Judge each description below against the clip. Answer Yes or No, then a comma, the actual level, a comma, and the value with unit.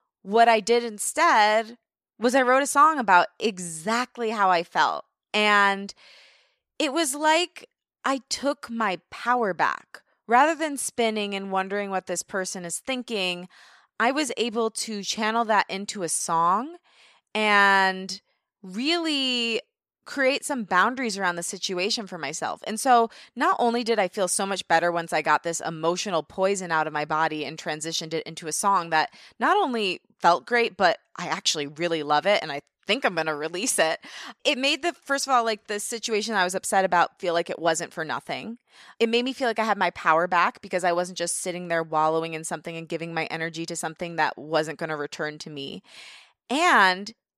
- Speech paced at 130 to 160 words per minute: No, average, 190 wpm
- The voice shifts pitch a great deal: Yes, wide, 5.7 semitones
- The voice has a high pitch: Yes, high, 195 Hz